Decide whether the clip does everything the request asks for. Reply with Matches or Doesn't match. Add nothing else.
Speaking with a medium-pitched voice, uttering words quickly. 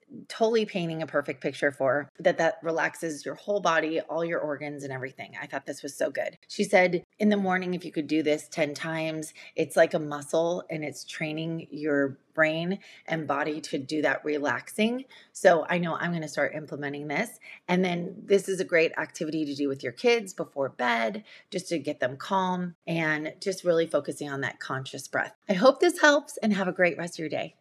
Matches